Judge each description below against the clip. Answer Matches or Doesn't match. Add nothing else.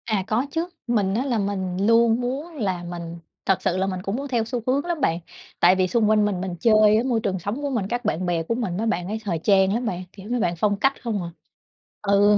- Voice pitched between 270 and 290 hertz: Doesn't match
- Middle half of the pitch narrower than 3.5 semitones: Doesn't match